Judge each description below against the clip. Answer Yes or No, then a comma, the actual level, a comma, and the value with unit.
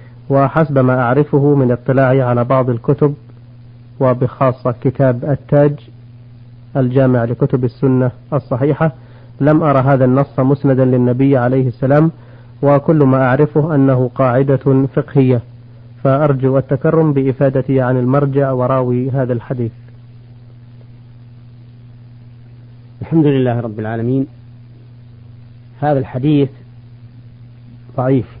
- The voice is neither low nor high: No, low, 130 Hz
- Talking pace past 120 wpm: No, average, 95 wpm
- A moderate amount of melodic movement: No, narrow, 2.3 semitones